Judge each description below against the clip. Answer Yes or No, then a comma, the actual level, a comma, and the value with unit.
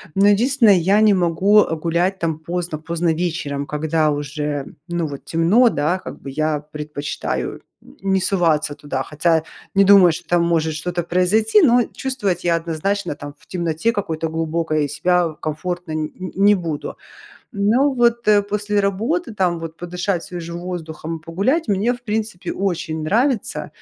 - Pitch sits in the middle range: Yes, medium, 175 Hz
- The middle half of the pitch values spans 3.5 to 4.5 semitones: Yes, average, 4.2 semitones